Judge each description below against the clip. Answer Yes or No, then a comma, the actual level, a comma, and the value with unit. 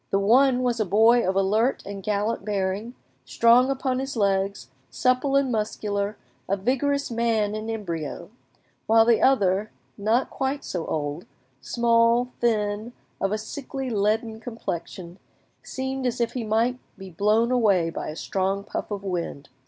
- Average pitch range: Yes, average, 3.7 semitones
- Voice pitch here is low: No, high, 220 Hz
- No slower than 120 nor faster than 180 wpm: Yes, average, 150 wpm